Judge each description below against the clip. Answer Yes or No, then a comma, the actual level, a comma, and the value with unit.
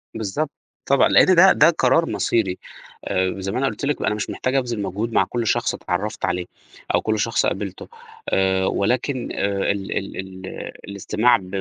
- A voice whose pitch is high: No, low, 105 Hz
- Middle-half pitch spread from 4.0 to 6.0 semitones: Yes, average, 5.1 semitones